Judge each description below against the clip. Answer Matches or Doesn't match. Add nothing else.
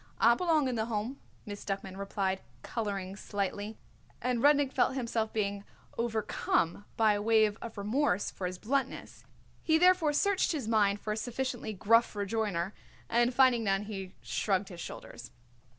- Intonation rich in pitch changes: Doesn't match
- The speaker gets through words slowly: Doesn't match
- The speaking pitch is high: Matches